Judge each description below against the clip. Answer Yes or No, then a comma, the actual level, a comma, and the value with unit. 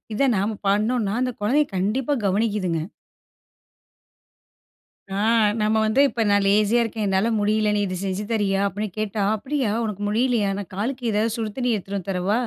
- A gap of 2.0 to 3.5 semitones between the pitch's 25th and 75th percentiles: Yes, narrow, 2.5 semitones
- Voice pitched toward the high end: Yes, high, 210 Hz